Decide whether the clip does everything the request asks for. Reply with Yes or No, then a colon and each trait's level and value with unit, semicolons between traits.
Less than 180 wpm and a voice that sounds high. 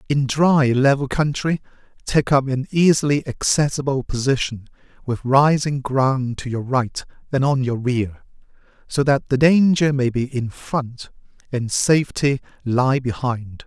No: average, 140 wpm; low, 135 Hz